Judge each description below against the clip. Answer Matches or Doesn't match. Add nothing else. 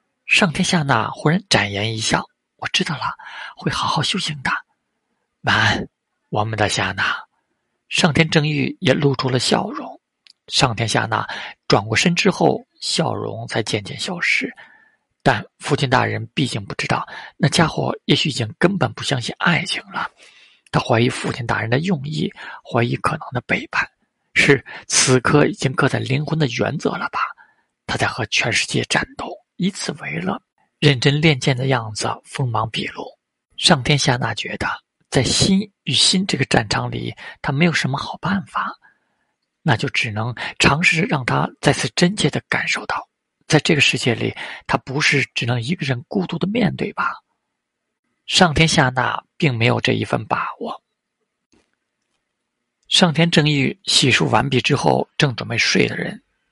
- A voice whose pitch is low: Doesn't match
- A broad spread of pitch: Matches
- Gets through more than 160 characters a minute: Matches